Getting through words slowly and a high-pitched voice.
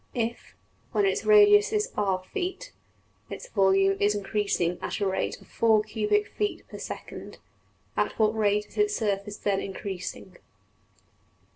Yes: slow, 130 wpm; high, 210 Hz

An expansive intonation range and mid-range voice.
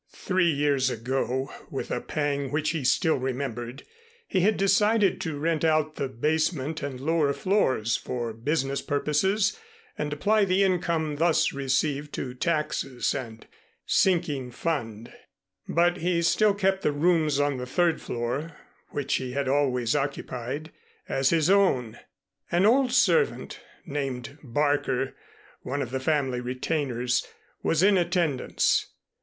No: average, 4.5 semitones; medium, 145 Hz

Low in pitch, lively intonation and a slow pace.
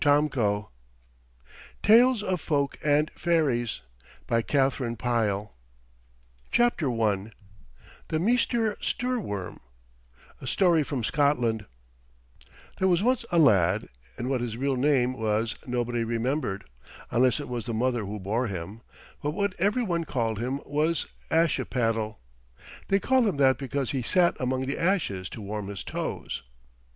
Yes: low, 130 Hz; wide, 6.4 semitones; slow, 125 wpm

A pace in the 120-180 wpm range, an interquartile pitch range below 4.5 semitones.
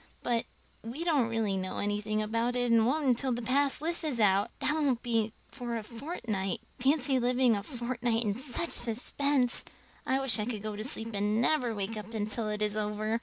No: average, 200 wpm; average, 3.3 semitones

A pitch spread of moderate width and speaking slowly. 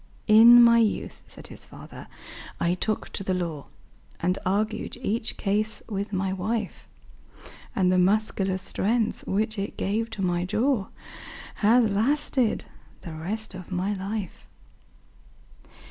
Yes: average, 3.0 semitones; slow, 130 wpm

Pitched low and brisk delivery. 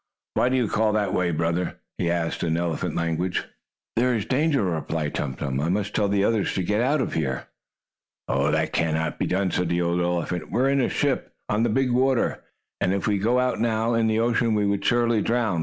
Yes: low, 100 Hz; fast, 225 wpm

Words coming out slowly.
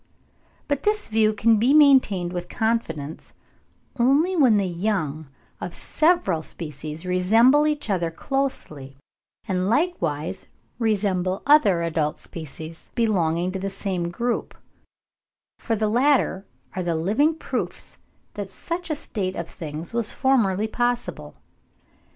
Yes: slow, 125 wpm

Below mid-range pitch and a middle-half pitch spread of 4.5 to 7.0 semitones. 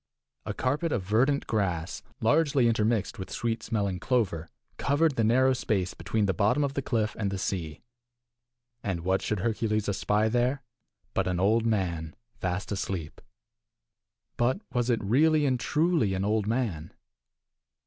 Yes: low, 110 Hz; average, 4.9 semitones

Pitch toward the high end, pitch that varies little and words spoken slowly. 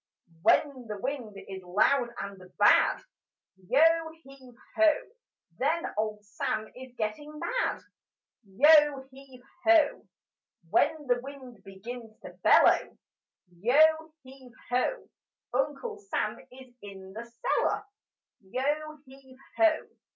No: very high, 260 Hz; average, 5.3 semitones; slow, 110 wpm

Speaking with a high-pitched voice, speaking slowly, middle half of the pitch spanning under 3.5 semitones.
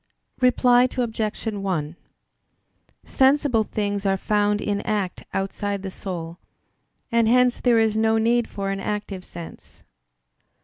Yes: high, 210 Hz; slow, 125 wpm; average, 2.9 semitones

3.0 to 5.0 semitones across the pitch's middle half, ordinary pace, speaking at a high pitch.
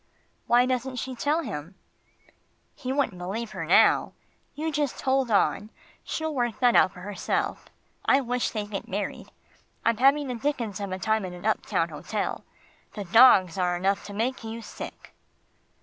Yes: average, 4.7 semitones; average, 165 wpm; high, 230 Hz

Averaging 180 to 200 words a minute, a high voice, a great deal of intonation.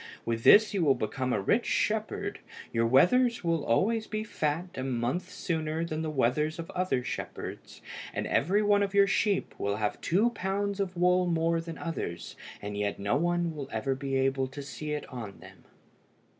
No: average, 185 wpm; medium, 155 Hz; wide, 6.0 semitones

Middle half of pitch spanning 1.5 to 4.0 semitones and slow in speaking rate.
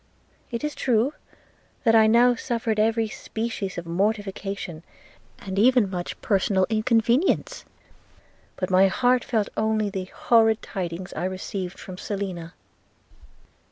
Yes: average, 3.5 semitones; slow, 125 wpm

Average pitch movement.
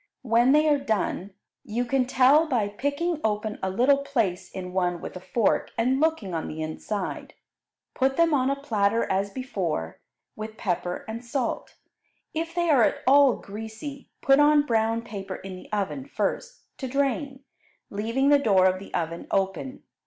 No: wide, 5.9 semitones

